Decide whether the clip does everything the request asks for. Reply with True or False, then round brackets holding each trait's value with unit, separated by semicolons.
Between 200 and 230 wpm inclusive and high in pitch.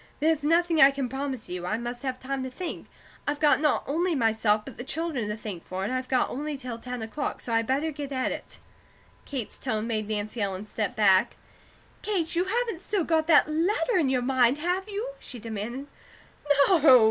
True (205 wpm; 265 Hz)